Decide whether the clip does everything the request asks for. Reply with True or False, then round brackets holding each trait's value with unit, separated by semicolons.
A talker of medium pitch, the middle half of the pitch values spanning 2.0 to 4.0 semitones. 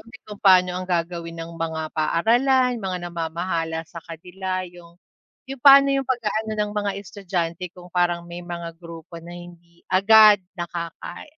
True (175 Hz; 3.6 semitones)